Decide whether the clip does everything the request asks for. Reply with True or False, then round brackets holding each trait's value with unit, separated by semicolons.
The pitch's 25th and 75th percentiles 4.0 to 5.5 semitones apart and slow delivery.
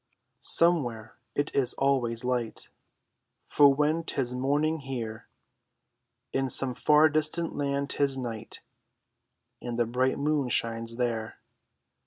False (3.5 semitones; 115 wpm)